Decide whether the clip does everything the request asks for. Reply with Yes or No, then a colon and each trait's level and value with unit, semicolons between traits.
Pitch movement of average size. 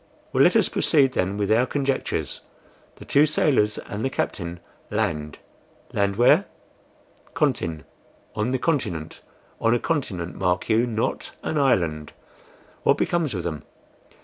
No: wide, 7.3 semitones